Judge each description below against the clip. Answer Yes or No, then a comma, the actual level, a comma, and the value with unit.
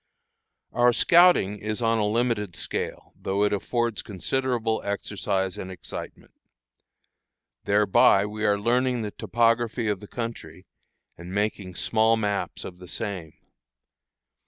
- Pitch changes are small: No, average, 3.0 semitones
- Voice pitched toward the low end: Yes, low, 105 Hz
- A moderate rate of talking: No, slow, 125 wpm